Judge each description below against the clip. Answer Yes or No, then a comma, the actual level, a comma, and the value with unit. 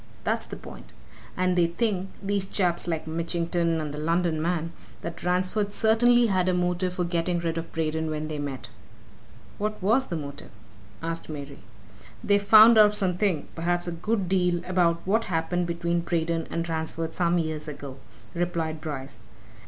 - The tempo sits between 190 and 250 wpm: No, average, 165 wpm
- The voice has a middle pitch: Yes, medium, 170 Hz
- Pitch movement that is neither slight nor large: No, narrow, 2.3 semitones